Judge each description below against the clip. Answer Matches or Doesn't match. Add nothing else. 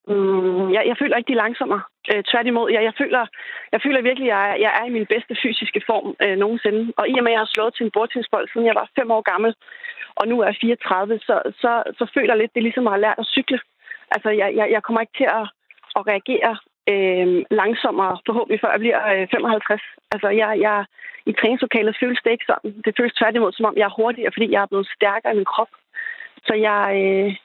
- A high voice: Matches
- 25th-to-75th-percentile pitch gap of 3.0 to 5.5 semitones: Doesn't match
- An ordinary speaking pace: Doesn't match